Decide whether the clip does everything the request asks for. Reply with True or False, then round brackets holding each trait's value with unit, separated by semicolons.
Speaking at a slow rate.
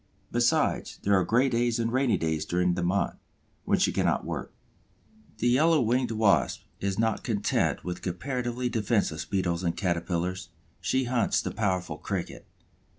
False (150 wpm)